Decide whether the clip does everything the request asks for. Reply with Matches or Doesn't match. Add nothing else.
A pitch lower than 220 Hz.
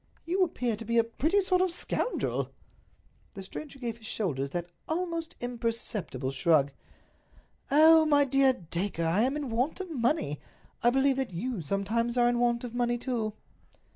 Doesn't match